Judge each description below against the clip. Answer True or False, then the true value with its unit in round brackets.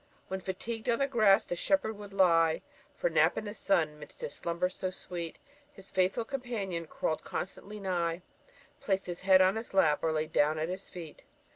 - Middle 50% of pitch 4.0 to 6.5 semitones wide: False (3.6 semitones)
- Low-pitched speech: False (185 Hz)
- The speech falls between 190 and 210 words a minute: True (195 wpm)